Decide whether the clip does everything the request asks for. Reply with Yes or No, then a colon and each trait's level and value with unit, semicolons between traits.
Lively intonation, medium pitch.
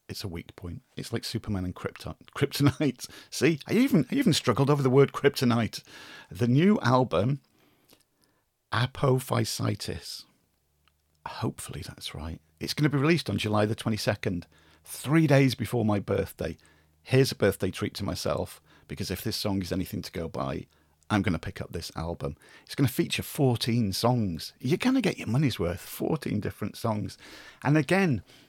No: wide, 7.1 semitones; low, 115 Hz